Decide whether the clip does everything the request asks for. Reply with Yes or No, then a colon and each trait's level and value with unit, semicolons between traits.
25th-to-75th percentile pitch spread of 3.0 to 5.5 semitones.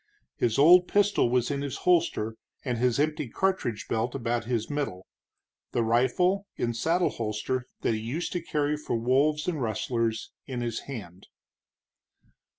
Yes: average, 4.8 semitones